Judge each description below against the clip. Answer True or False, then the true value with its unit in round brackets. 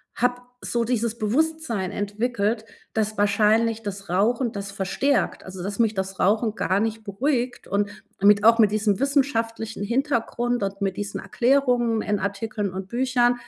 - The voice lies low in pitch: False (220 Hz)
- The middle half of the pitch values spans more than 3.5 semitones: False (3.2 semitones)